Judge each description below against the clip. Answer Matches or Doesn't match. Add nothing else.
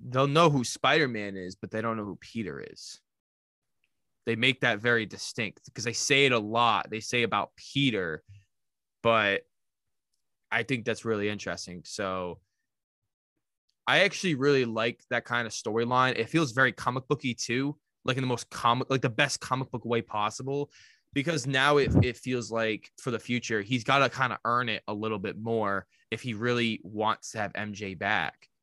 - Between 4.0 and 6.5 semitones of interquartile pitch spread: Doesn't match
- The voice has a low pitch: Matches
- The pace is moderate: Matches